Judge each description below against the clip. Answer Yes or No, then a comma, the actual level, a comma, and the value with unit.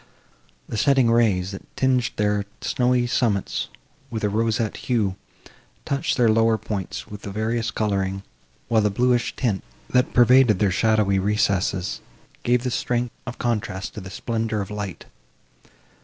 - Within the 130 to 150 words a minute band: Yes, average, 140 wpm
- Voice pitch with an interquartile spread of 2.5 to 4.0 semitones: Yes, average, 3.3 semitones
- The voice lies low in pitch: Yes, low, 110 Hz